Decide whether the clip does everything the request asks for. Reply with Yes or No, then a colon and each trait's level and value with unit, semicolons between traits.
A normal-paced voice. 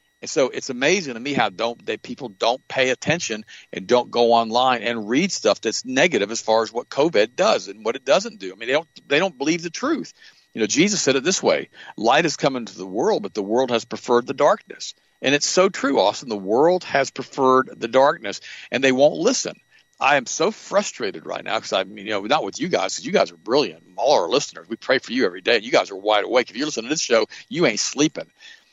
No: fast, 255 wpm